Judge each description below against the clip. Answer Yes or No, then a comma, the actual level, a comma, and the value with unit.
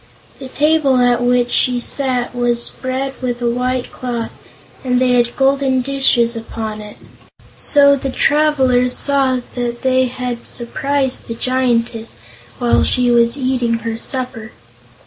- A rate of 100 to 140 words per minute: Yes, slow, 135 wpm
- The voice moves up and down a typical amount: No, narrow, 1.7 semitones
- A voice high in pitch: Yes, very high, 250 Hz